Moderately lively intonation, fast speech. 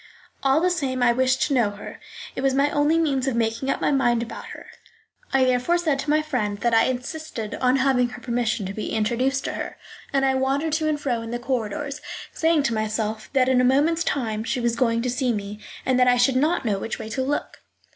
Yes: average, 3.1 semitones; fast, 235 wpm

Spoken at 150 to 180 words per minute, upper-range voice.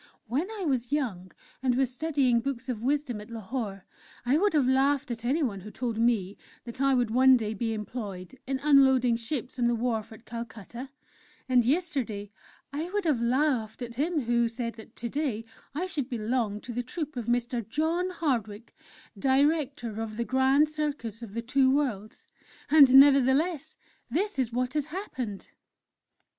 Yes: average, 170 wpm; very high, 250 Hz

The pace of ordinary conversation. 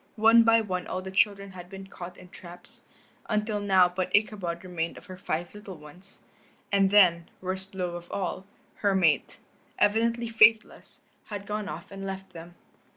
Yes: average, 170 wpm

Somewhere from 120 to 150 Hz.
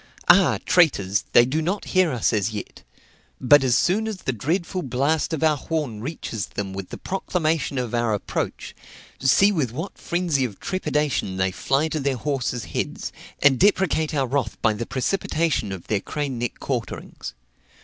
Yes: medium, 140 Hz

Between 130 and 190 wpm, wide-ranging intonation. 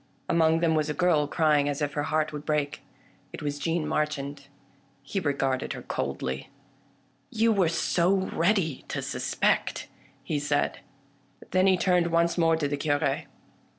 No: average, 160 wpm; average, 2.7 semitones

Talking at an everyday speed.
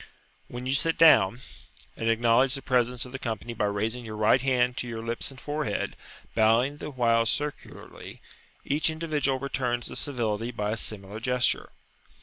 Yes: average, 165 wpm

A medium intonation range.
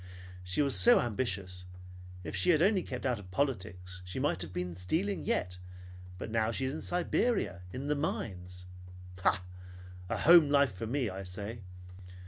No: wide, 7.7 semitones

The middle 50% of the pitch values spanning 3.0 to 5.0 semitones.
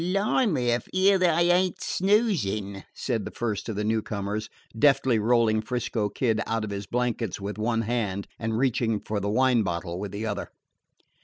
Yes: average, 4.1 semitones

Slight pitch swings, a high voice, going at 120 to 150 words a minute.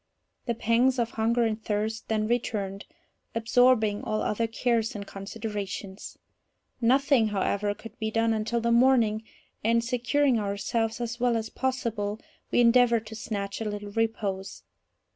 Yes: narrow, 2.1 semitones; high, 225 Hz; average, 145 wpm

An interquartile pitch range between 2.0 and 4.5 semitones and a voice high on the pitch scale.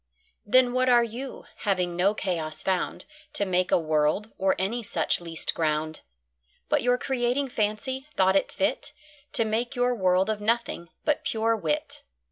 No: average, 5.2 semitones; high, 210 Hz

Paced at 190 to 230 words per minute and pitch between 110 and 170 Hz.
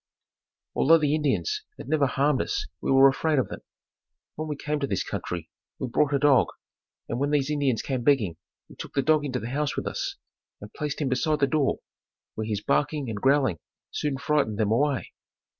Yes: average, 200 wpm; medium, 140 Hz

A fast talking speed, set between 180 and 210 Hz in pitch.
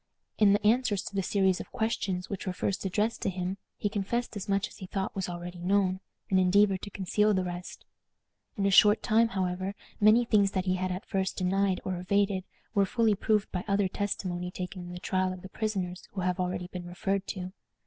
Yes: fast, 215 wpm; high, 190 Hz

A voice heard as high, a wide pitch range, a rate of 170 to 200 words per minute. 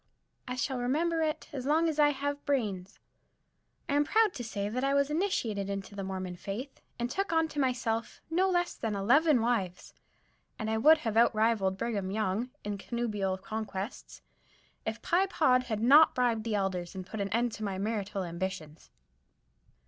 Yes: high, 230 Hz; wide, 6.3 semitones; average, 175 wpm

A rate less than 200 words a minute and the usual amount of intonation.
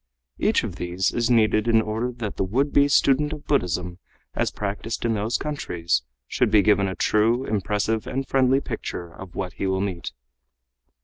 Yes: average, 180 wpm; average, 4.6 semitones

